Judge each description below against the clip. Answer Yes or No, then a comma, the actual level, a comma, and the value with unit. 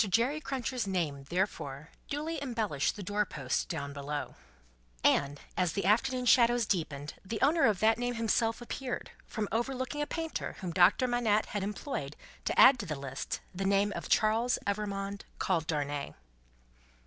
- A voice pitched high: Yes, high, 205 Hz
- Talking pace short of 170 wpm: Yes, average, 155 wpm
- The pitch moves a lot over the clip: Yes, wide, 6.7 semitones